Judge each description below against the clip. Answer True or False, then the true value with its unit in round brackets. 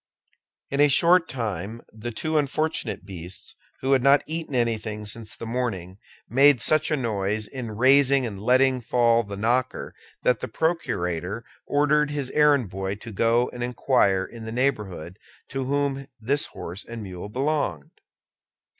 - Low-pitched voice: True (120 Hz)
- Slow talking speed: False (155 wpm)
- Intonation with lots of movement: False (4.8 semitones)